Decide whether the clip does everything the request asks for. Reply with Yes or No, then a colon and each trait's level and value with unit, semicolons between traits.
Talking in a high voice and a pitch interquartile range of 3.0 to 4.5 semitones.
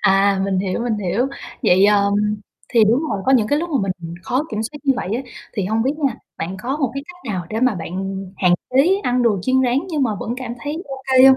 No: high, 235 Hz; average, 5.1 semitones